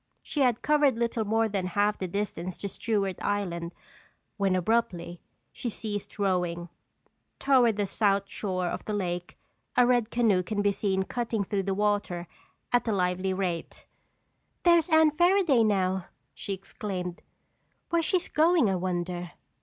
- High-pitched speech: Yes, high, 205 Hz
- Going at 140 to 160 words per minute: Yes, average, 150 wpm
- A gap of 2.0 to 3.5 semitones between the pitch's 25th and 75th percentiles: No, average, 4.2 semitones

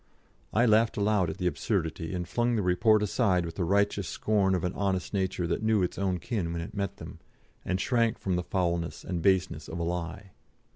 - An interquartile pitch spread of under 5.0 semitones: Yes, average, 3.0 semitones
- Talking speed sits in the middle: No, fast, 210 wpm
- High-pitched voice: No, very low, 95 Hz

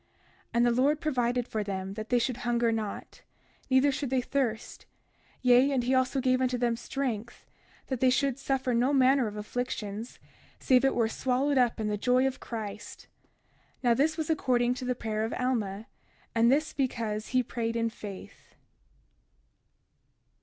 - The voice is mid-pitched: No, high, 245 Hz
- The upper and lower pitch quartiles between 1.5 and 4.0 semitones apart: Yes, narrow, 2.5 semitones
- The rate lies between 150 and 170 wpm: Yes, average, 165 wpm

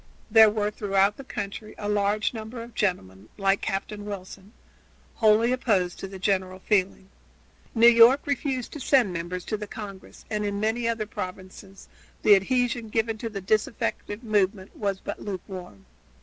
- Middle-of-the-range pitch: No, high, 210 Hz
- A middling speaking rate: Yes, average, 160 wpm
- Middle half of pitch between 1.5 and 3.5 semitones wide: Yes, narrow, 2.6 semitones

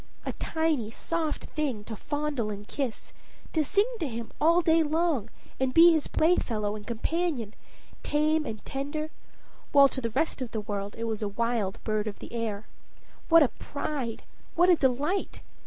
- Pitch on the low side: No, very high, 270 Hz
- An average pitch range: No, wide, 6.2 semitones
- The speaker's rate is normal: Yes, average, 170 wpm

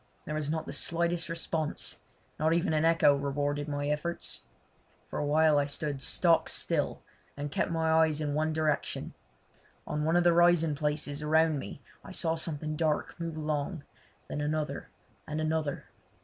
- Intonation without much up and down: Yes, narrow, 1.8 semitones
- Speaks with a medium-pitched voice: Yes, medium, 155 Hz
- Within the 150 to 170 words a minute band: Yes, average, 165 wpm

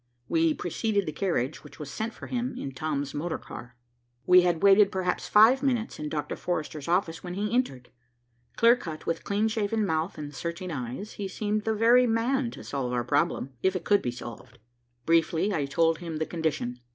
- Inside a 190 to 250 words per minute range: Yes, average, 195 wpm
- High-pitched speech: No, medium, 175 Hz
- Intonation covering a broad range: Yes, wide, 5.7 semitones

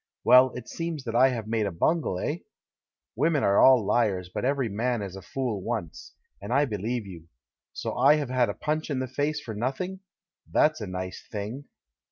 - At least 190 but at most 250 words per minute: Yes, average, 200 wpm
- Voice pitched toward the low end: Yes, low, 120 Hz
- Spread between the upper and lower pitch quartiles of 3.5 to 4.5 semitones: No, average, 5.2 semitones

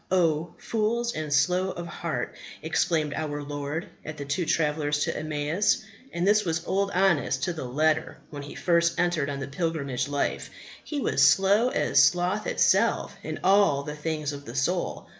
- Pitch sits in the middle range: Yes, medium, 160 Hz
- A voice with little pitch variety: No, average, 3.8 semitones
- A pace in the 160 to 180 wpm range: Yes, average, 170 wpm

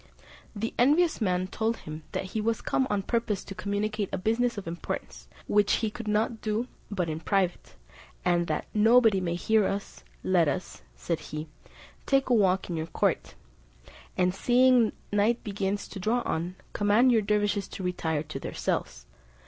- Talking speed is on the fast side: No, average, 175 wpm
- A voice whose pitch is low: No, high, 205 Hz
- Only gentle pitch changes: No, average, 3.7 semitones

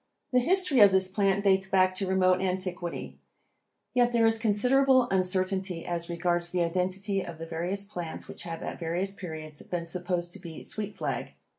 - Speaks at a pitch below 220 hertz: Yes, medium, 185 Hz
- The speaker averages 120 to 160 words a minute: No, average, 175 wpm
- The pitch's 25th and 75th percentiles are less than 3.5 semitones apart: Yes, narrow, 2.5 semitones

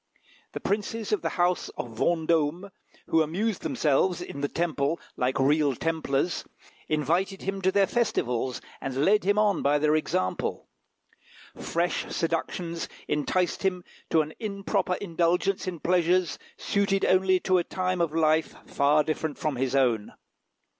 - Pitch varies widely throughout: No, average, 4.0 semitones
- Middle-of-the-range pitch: Yes, medium, 170 Hz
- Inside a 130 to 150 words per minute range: Yes, average, 145 wpm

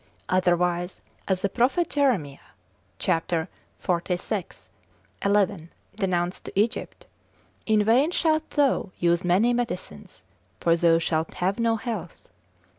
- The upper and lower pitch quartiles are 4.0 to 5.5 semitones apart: Yes, average, 4.9 semitones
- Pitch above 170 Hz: Yes, high, 190 Hz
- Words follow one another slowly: Yes, slow, 115 wpm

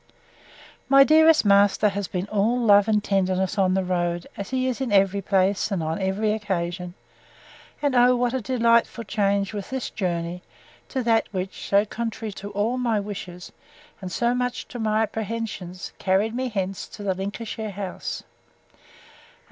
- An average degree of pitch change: Yes, average, 3.4 semitones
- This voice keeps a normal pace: Yes, average, 165 wpm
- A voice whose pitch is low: No, high, 205 Hz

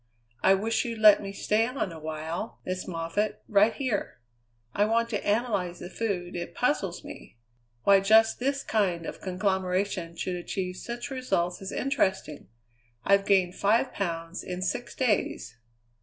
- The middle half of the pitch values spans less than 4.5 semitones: Yes, average, 3.7 semitones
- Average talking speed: Yes, average, 155 wpm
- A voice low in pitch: No, high, 195 Hz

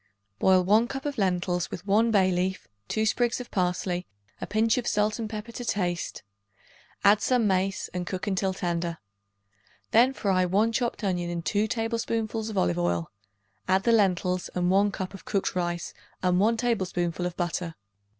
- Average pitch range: Yes, average, 3.7 semitones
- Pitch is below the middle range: No, high, 195 Hz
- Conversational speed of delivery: Yes, average, 175 wpm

